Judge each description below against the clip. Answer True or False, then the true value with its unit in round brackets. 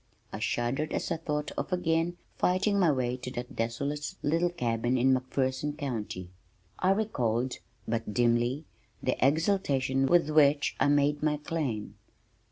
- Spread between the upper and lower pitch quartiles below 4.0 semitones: False (4.7 semitones)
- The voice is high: False (140 Hz)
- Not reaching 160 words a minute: True (150 wpm)